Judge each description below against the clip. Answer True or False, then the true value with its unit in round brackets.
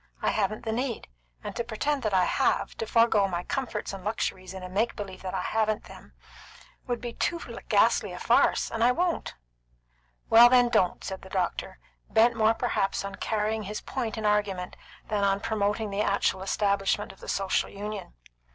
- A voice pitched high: True (210 Hz)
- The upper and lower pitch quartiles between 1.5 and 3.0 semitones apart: True (2.7 semitones)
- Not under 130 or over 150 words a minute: False (190 wpm)